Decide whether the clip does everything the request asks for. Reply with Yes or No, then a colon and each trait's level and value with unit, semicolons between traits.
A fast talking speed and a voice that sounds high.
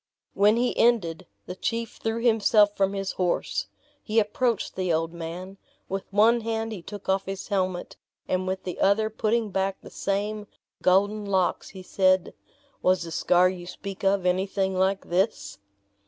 No: average, 165 wpm; high, 195 Hz